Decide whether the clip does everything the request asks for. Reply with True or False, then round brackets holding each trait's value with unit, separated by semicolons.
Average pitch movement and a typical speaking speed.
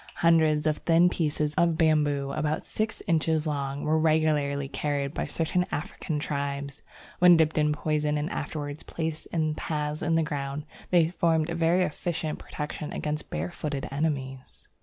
False (1.8 semitones; 155 wpm)